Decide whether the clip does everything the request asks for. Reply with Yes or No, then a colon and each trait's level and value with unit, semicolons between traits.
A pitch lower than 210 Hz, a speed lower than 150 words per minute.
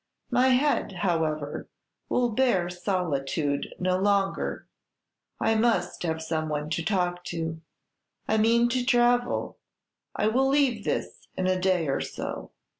Yes: medium, 185 Hz; slow, 135 wpm